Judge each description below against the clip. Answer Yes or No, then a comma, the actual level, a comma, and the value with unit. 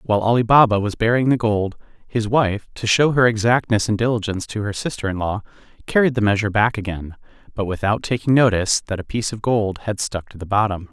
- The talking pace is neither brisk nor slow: No, fast, 215 wpm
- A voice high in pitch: No, low, 110 Hz